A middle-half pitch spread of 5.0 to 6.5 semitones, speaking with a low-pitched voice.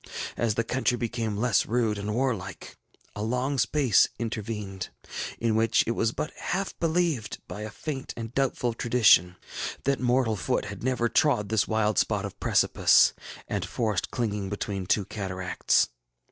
No: average, 3.1 semitones; low, 115 Hz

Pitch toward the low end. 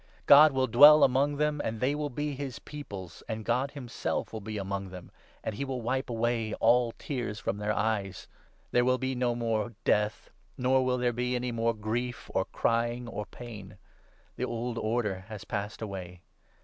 Yes: low, 120 Hz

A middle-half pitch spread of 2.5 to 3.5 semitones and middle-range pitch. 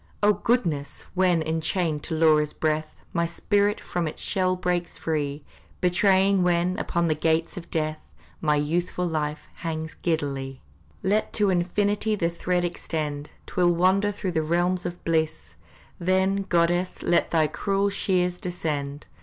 Yes: average, 2.8 semitones; medium, 175 Hz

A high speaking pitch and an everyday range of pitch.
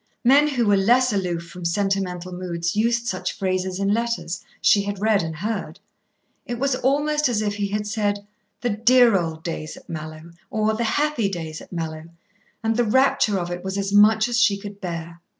Yes: high, 205 Hz; average, 4.7 semitones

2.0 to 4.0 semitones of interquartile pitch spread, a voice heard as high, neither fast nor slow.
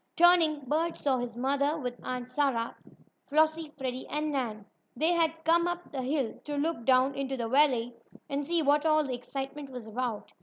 Yes: average, 3.6 semitones; very high, 280 Hz; average, 185 wpm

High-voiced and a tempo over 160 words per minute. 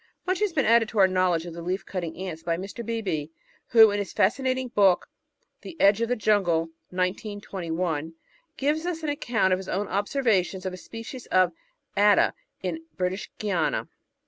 Yes: high, 200 Hz; average, 175 wpm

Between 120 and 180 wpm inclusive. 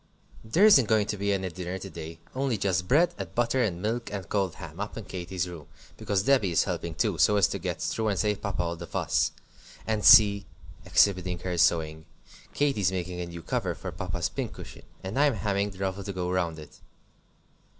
No: average, 200 wpm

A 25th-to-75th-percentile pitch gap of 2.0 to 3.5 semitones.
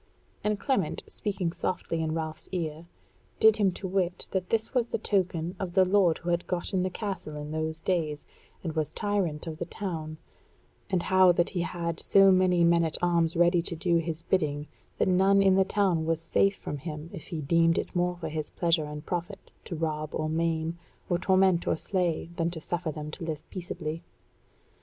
Yes: average, 2.8 semitones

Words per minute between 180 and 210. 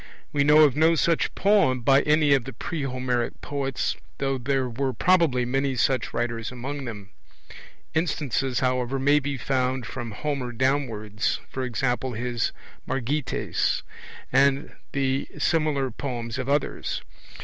No: slow, 135 wpm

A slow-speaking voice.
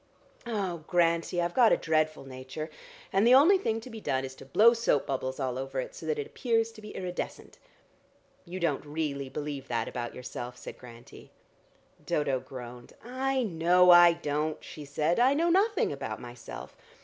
No: average, 180 wpm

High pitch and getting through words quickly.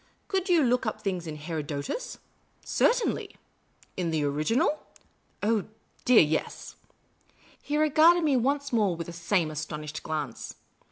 No: high, 195 Hz; average, 160 wpm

